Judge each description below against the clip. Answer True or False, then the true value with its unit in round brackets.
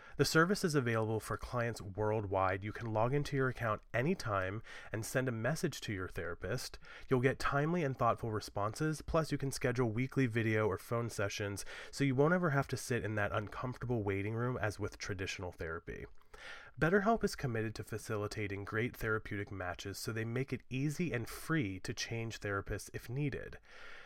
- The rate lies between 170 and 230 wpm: True (180 wpm)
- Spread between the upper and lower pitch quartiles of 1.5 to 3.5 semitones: False (4.6 semitones)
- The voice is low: True (115 Hz)